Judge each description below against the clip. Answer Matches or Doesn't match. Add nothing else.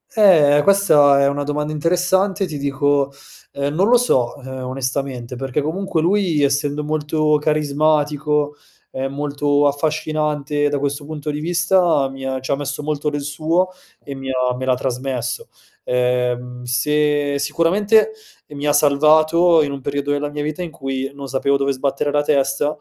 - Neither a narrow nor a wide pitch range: Doesn't match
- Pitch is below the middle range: Doesn't match